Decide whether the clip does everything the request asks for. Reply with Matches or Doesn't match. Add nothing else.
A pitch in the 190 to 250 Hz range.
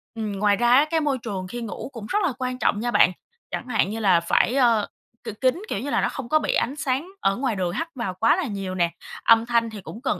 Matches